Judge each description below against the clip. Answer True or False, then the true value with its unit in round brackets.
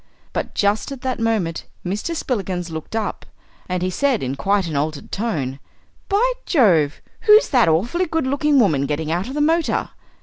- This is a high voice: True (205 Hz)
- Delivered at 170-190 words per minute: True (175 wpm)